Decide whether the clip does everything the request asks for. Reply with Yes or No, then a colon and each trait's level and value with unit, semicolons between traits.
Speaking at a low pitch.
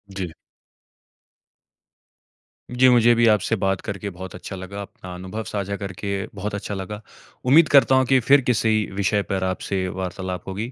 Yes: low, 100 Hz